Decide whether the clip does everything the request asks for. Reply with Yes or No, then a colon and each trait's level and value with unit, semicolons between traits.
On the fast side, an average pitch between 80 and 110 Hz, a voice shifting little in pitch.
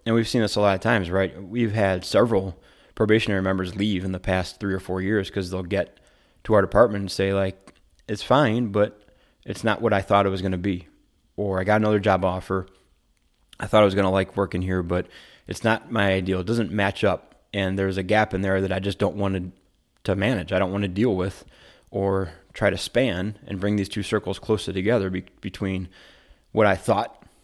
Yes: fast, 225 wpm; low, 100 Hz; narrow, 1.8 semitones